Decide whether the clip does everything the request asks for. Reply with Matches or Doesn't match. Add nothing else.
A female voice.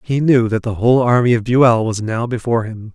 Doesn't match